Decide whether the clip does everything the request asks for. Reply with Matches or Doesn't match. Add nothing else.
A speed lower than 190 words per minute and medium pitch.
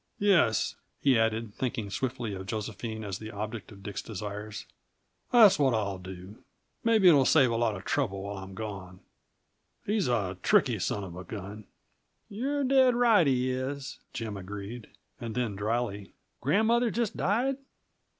Doesn't match